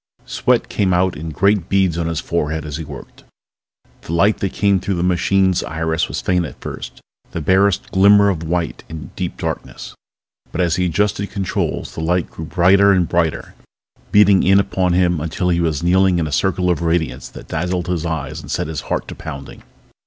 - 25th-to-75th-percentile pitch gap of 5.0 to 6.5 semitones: No, average, 2.8 semitones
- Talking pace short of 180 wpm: No, average, 195 wpm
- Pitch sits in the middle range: No, very low, 90 Hz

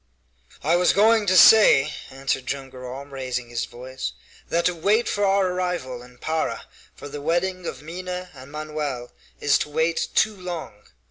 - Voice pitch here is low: No, medium, 155 Hz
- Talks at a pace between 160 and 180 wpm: Yes, average, 170 wpm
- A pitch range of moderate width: No, wide, 5.7 semitones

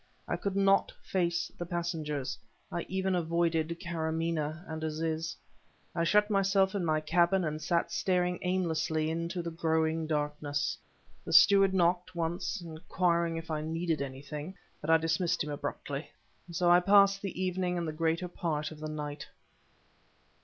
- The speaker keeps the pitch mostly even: Yes, narrow, 2.3 semitones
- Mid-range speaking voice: Yes, medium, 170 Hz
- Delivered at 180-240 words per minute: No, average, 155 wpm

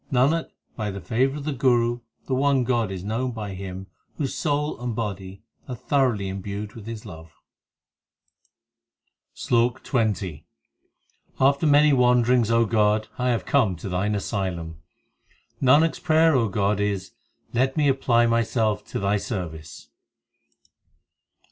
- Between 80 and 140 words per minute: Yes, slow, 135 wpm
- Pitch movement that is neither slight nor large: Yes, average, 4.7 semitones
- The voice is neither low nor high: No, low, 115 Hz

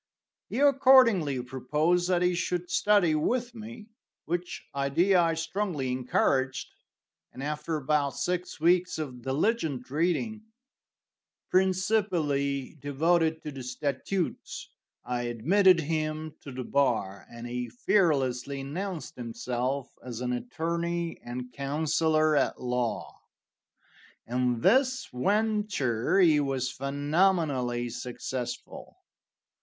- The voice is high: No, medium, 150 Hz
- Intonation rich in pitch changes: Yes, wide, 5.8 semitones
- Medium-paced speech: No, slow, 105 wpm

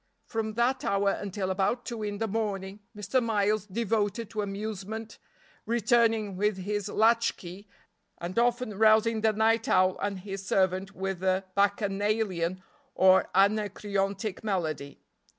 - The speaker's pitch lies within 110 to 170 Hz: No, high, 205 Hz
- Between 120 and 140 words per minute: Yes, slow, 135 wpm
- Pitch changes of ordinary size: No, narrow, 2.3 semitones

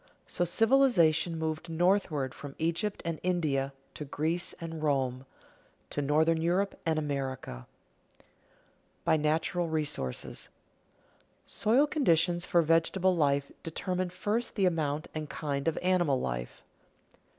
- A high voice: No, medium, 160 Hz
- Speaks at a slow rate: Yes, slow, 120 wpm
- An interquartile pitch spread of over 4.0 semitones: No, average, 3.4 semitones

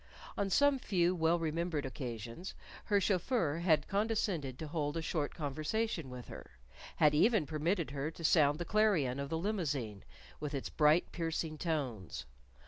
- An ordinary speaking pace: Yes, average, 155 wpm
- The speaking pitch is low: No, medium, 160 Hz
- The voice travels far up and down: No, average, 4.0 semitones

